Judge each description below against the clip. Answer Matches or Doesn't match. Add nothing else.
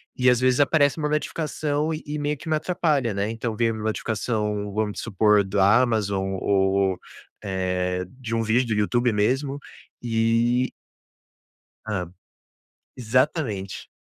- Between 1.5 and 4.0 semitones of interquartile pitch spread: Doesn't match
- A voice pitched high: Doesn't match